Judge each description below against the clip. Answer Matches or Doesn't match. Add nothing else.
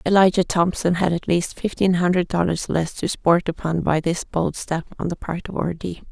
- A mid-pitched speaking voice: Matches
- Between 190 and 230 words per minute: Matches